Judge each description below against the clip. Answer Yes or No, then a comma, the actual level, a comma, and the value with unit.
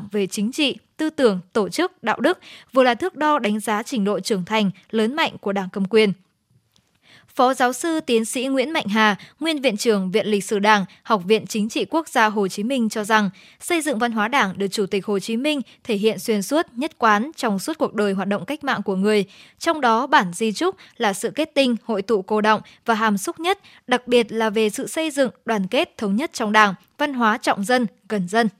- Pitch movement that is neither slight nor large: Yes, average, 4.3 semitones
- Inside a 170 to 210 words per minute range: No, average, 240 wpm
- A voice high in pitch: Yes, high, 225 Hz